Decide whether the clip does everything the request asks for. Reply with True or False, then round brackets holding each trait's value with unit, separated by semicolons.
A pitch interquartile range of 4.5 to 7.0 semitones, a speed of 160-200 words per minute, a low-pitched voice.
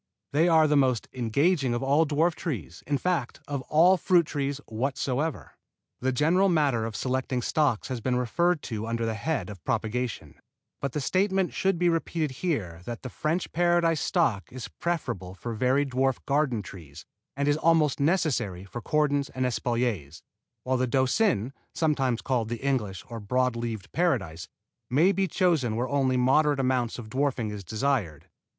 True (4.9 semitones; 170 wpm; 130 Hz)